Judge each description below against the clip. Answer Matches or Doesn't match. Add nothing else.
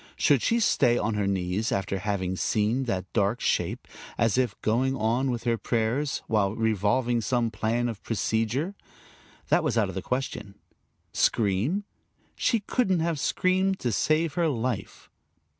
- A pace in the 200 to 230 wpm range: Doesn't match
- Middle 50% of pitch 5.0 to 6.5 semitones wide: Doesn't match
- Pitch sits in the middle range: Doesn't match